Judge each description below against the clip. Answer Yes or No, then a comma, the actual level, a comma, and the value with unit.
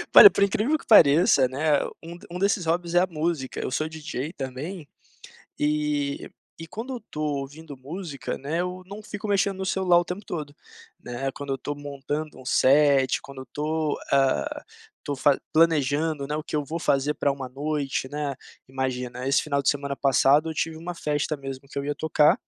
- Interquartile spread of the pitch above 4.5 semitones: No, average, 3.4 semitones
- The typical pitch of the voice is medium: Yes, medium, 150 Hz